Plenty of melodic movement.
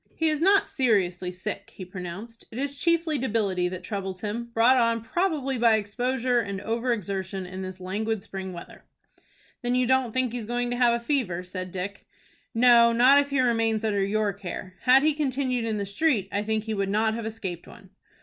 No: average, 4.3 semitones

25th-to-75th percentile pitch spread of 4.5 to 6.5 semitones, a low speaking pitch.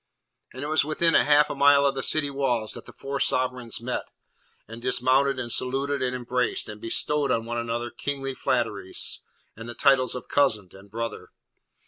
No: average, 3.0 semitones; low, 130 Hz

